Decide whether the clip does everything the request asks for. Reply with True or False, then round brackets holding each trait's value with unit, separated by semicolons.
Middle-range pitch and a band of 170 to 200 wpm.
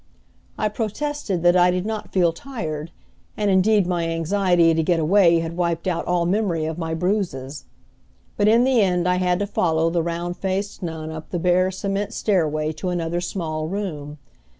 True (175 Hz; 180 wpm)